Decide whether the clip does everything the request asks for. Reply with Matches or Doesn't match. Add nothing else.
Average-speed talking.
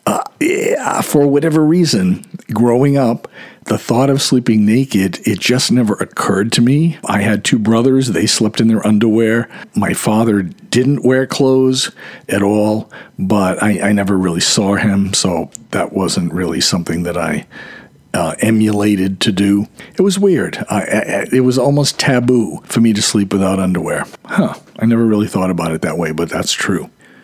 Matches